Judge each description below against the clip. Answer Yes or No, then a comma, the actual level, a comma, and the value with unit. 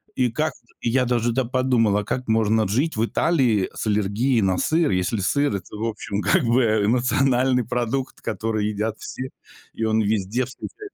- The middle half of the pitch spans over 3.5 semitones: No, average, 3.2 semitones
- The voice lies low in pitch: Yes, low, 115 Hz